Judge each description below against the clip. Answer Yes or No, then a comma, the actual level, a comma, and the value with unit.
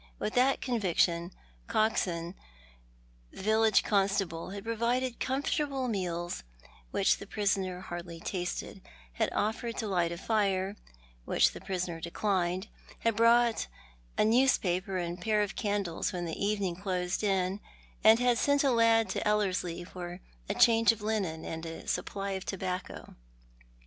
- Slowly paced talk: No, average, 145 wpm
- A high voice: Yes, high, 195 Hz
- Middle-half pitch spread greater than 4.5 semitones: No, average, 3.9 semitones